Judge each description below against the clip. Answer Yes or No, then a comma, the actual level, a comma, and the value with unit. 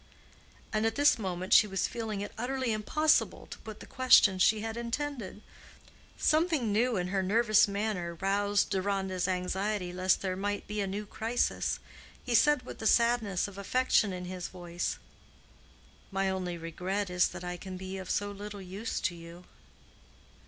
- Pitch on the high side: Yes, high, 200 Hz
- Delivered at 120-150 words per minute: No, average, 165 wpm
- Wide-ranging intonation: No, average, 3.2 semitones